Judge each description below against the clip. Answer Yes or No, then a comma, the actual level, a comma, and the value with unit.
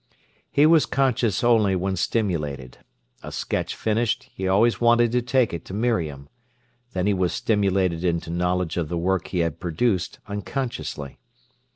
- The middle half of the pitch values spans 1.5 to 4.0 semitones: No, average, 5.3 semitones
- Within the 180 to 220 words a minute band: No, average, 155 wpm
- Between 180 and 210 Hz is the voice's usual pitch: No, very low, 95 Hz